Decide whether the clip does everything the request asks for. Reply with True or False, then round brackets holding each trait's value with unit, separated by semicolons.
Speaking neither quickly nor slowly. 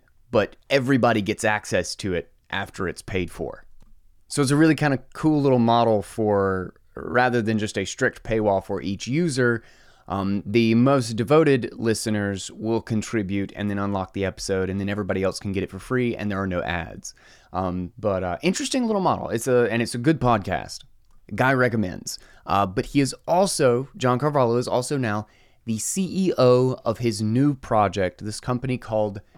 True (180 wpm)